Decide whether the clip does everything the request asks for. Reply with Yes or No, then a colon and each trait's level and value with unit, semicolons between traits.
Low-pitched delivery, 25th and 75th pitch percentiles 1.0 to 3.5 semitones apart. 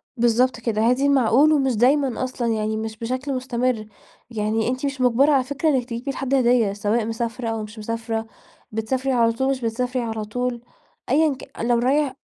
No: high, 245 Hz; average, 2.7 semitones